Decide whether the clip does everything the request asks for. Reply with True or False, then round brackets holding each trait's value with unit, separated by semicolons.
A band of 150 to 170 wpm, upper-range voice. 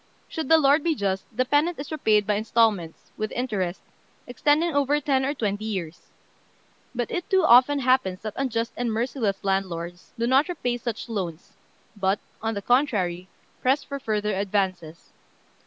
True (160 wpm; 230 Hz)